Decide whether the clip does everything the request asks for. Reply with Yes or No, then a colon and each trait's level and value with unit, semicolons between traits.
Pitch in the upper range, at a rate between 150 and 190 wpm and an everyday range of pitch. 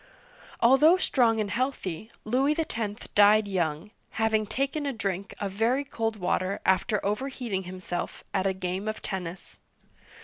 No: high, 215 Hz; average, 140 wpm; average, 4.5 semitones